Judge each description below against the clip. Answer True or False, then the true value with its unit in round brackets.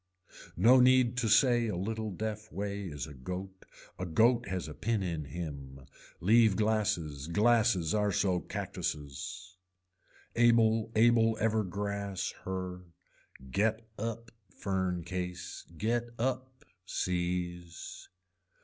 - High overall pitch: False (100 Hz)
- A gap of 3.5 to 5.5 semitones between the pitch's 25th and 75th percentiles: True (4.2 semitones)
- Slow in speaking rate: True (115 wpm)